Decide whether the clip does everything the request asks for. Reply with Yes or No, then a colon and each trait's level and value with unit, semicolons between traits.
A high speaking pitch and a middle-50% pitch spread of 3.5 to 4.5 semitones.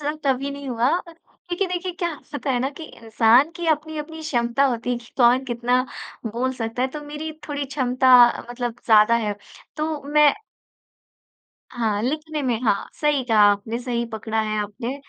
Yes: very high, 260 Hz; average, 4.2 semitones